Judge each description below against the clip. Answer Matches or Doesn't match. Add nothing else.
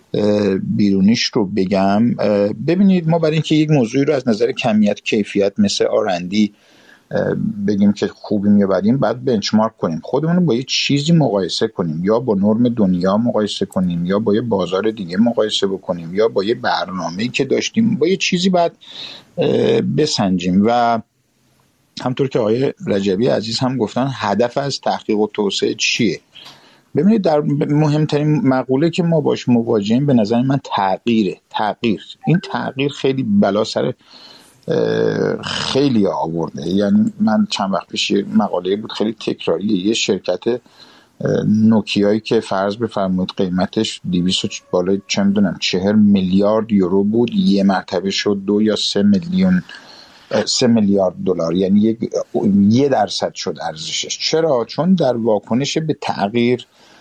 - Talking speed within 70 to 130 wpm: Doesn't match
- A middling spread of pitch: Doesn't match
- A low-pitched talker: Matches